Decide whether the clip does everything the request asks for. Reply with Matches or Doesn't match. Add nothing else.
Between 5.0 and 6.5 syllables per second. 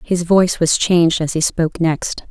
Matches